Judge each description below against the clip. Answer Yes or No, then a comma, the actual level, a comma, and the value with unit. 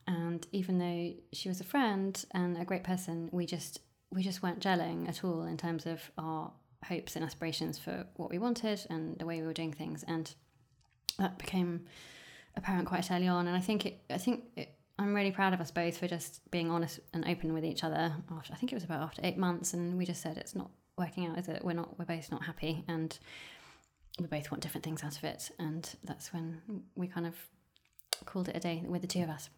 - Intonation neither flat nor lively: No, narrow, 2.0 semitones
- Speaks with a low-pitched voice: No, medium, 170 Hz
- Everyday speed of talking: No, fast, 235 wpm